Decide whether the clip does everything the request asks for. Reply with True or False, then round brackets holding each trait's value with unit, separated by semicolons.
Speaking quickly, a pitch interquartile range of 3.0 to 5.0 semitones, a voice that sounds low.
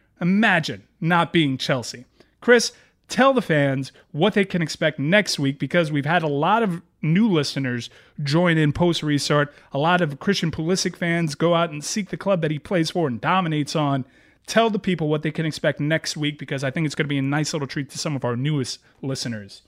False (215 wpm; 3.6 semitones; 155 Hz)